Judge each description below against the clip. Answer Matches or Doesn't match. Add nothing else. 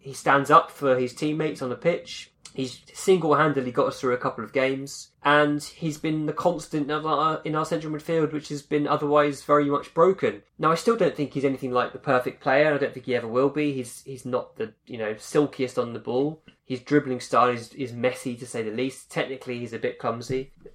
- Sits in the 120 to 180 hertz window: Matches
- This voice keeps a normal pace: Doesn't match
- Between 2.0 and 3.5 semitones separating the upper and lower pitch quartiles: Matches